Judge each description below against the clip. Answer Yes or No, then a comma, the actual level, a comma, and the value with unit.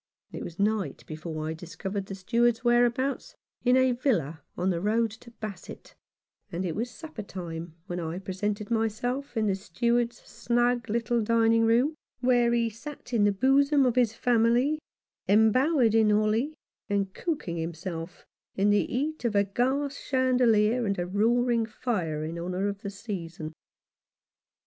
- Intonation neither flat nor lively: Yes, average, 4.1 semitones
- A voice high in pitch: Yes, high, 225 Hz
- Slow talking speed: No, average, 155 wpm